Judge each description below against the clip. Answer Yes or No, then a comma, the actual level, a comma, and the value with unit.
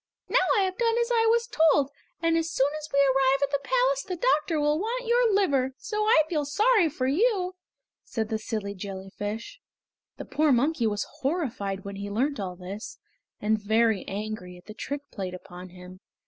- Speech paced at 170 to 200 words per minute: Yes, average, 190 wpm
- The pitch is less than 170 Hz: No, very high, 275 Hz